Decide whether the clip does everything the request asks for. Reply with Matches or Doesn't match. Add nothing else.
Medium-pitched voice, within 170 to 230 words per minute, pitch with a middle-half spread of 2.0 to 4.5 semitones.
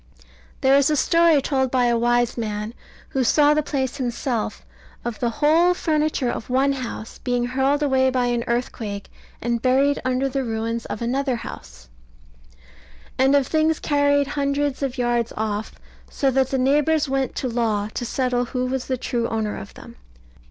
Doesn't match